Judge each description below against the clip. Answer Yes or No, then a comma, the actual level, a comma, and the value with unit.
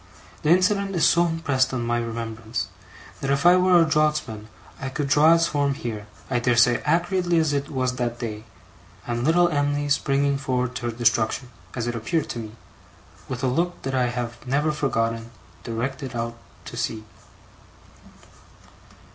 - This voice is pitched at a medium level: No, low, 130 Hz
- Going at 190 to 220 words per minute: No, average, 170 wpm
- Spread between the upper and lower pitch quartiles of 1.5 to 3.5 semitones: No, average, 4.3 semitones